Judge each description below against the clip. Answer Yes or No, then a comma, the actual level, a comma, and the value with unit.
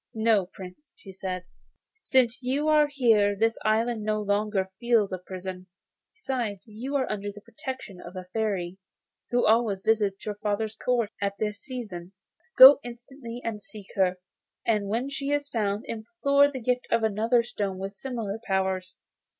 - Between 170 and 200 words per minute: No, average, 160 wpm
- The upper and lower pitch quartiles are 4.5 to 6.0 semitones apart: No, average, 3.7 semitones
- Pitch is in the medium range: No, high, 215 Hz